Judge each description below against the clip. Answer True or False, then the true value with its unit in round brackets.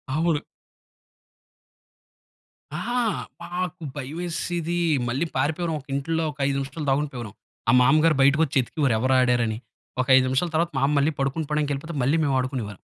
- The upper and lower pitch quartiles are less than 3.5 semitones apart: False (3.8 semitones)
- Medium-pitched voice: True (145 Hz)